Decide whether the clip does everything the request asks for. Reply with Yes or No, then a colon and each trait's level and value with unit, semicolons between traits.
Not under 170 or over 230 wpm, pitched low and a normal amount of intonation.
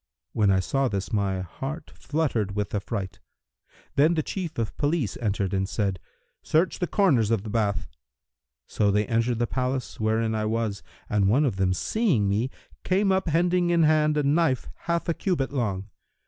No: average, 175 wpm; low, 115 Hz; wide, 7.3 semitones